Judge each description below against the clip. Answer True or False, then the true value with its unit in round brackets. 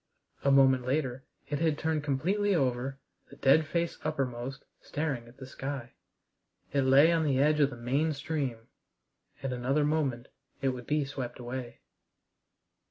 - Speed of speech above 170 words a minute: False (155 wpm)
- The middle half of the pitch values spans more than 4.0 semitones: False (3.1 semitones)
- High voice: False (135 Hz)